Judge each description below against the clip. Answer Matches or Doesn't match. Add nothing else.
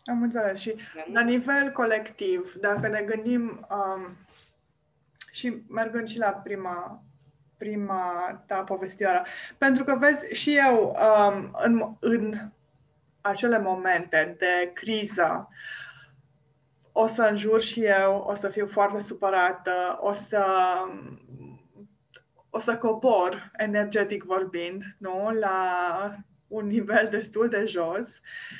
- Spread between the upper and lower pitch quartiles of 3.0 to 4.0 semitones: Matches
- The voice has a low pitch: Doesn't match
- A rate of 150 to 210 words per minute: Doesn't match